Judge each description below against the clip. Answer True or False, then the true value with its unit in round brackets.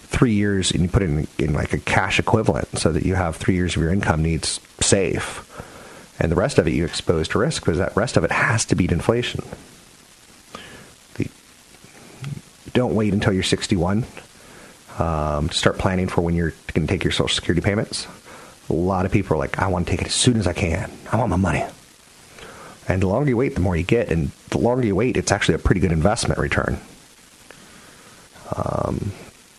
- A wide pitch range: False (4.0 semitones)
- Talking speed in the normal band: False (210 wpm)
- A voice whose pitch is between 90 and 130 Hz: True (95 Hz)